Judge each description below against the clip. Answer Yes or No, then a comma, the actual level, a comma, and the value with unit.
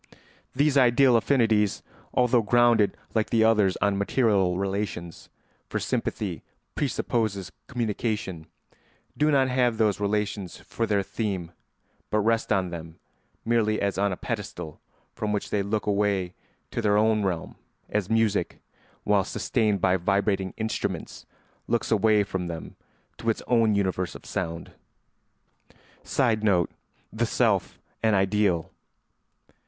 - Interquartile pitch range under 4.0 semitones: Yes, average, 2.9 semitones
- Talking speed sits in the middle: No, slow, 125 wpm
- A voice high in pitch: No, low, 105 Hz